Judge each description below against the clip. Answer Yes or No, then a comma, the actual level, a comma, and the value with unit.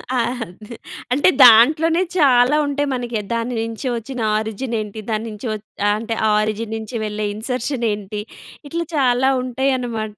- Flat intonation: No, average, 3.3 semitones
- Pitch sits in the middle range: No, high, 235 Hz